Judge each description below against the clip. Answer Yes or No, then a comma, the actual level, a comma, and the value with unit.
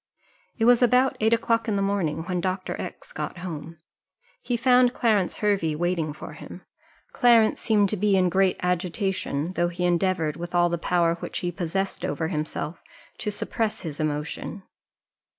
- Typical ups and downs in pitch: Yes, average, 3.9 semitones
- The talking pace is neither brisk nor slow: Yes, average, 170 wpm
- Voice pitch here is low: No, medium, 185 Hz